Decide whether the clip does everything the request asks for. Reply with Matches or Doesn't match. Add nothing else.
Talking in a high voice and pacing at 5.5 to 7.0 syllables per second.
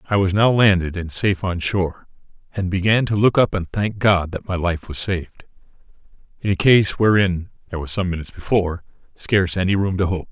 Doesn't match